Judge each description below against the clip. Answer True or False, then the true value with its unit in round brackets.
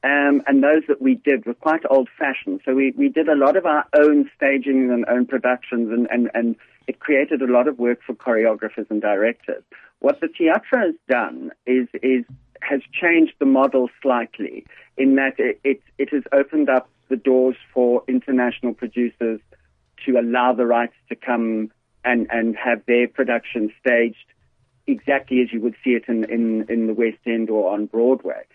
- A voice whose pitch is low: True (125 Hz)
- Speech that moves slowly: False (185 wpm)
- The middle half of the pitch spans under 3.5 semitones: True (2.7 semitones)